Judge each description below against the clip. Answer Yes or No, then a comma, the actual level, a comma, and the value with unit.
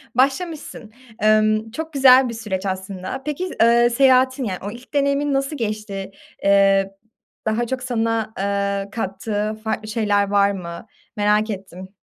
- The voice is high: Yes, high, 215 Hz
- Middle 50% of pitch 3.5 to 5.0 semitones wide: Yes, average, 4.2 semitones